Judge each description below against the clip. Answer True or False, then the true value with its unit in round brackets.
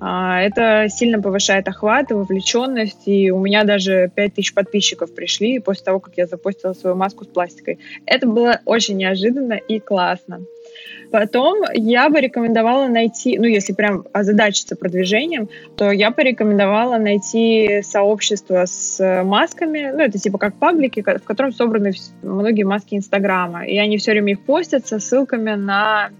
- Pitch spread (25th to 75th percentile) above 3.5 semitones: False (2.8 semitones)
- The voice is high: True (210 Hz)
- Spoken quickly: False (150 wpm)